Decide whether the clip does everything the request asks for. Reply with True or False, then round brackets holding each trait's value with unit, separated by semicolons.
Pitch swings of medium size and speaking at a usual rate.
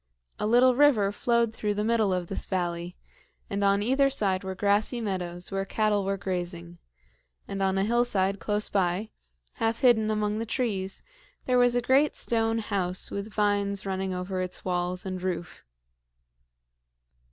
True (3.1 semitones; 160 wpm)